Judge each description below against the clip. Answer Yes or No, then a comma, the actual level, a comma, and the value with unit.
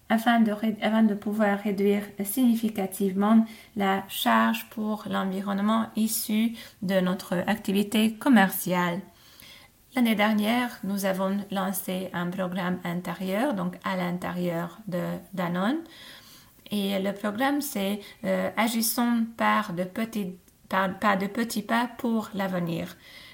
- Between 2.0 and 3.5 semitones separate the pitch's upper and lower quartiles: Yes, average, 2.8 semitones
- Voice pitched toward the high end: Yes, high, 200 Hz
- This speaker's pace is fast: No, average, 115 wpm